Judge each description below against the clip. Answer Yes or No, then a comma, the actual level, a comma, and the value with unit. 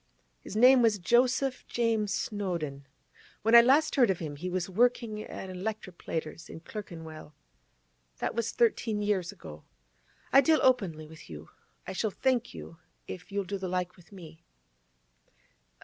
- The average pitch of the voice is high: Yes, high, 200 Hz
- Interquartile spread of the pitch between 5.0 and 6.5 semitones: Yes, wide, 5.5 semitones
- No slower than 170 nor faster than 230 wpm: No, average, 155 wpm